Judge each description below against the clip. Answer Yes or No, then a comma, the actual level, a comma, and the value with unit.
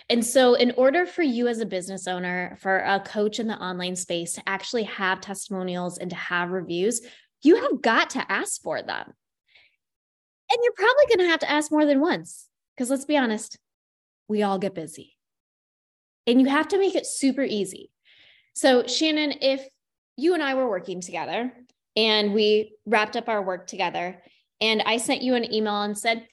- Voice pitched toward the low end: No, high, 220 Hz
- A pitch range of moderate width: No, wide, 5.9 semitones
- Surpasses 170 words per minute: Yes, average, 190 wpm